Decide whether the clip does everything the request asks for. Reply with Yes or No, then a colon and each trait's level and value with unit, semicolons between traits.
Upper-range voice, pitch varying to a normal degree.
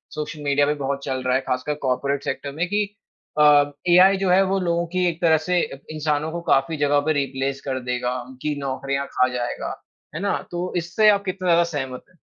No: medium, 150 Hz; average, 4.1 semitones